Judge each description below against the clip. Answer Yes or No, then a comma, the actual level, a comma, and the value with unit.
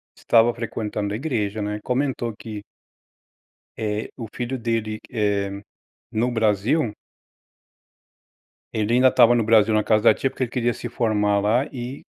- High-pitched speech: No, low, 115 Hz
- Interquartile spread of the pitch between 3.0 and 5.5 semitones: No, narrow, 2.4 semitones